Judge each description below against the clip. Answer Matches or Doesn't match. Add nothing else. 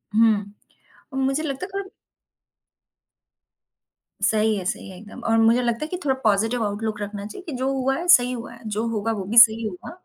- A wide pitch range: Doesn't match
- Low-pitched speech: Doesn't match